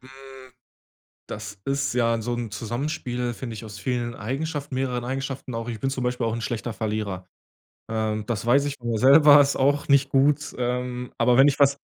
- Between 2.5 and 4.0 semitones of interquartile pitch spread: Yes, average, 2.9 semitones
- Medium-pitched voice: No, low, 125 Hz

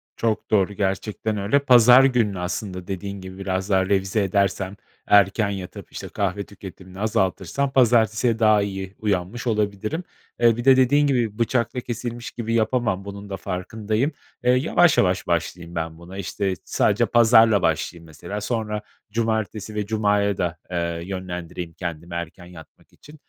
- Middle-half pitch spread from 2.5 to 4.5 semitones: Yes, average, 3.6 semitones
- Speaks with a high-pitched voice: No, low, 100 Hz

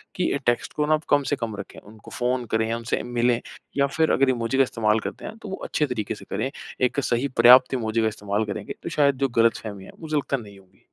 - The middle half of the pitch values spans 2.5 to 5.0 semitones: Yes, average, 3.9 semitones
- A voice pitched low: Yes, low, 120 Hz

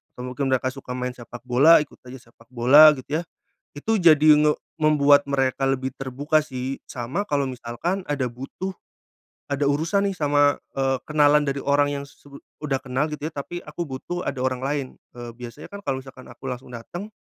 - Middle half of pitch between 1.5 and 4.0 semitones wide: Yes, average, 2.8 semitones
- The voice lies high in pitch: No, medium, 140 Hz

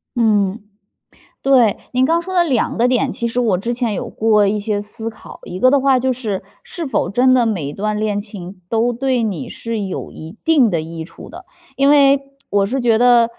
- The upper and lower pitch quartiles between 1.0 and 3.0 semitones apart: No, average, 4.0 semitones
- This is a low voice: No, high, 230 Hz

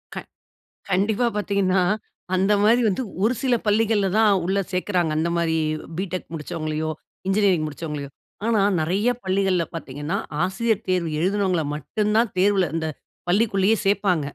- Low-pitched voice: No, high, 190 Hz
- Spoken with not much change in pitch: No, average, 3.6 semitones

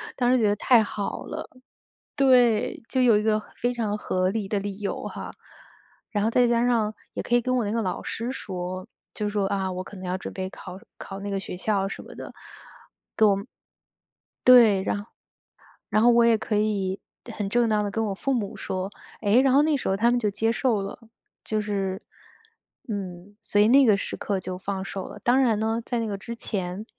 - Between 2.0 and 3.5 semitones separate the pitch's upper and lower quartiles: Yes, average, 3.2 semitones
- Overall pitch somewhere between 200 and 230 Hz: Yes, high, 210 Hz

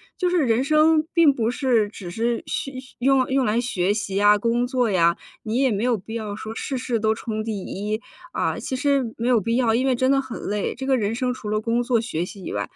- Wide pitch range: No, average, 3.4 semitones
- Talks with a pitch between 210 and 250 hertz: Yes, high, 230 Hz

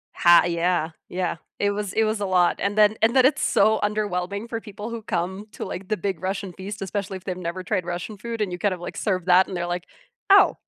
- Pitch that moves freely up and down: No, average, 2.9 semitones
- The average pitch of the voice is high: Yes, high, 195 Hz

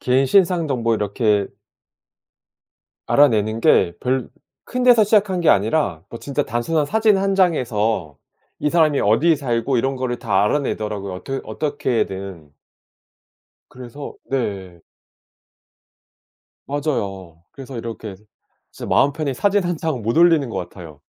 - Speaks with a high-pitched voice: No, low, 130 Hz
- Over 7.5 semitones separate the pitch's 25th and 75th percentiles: No, wide, 6.7 semitones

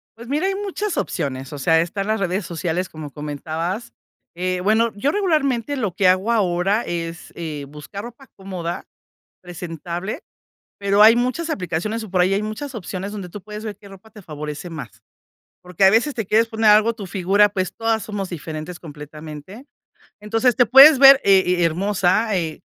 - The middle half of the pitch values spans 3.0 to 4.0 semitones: No, average, 4.7 semitones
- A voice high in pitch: Yes, high, 195 Hz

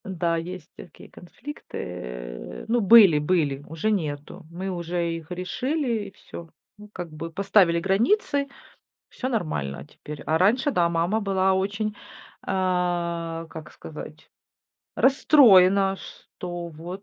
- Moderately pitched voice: Yes, medium, 180 Hz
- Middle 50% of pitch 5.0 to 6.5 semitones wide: No, average, 3.3 semitones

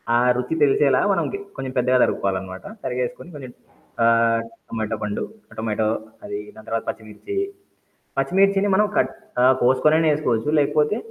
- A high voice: No, low, 125 Hz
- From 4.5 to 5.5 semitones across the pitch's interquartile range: Yes, average, 4.9 semitones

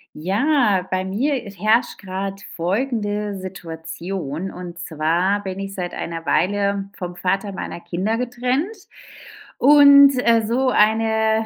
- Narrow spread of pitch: No, average, 4.1 semitones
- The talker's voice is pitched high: Yes, high, 200 Hz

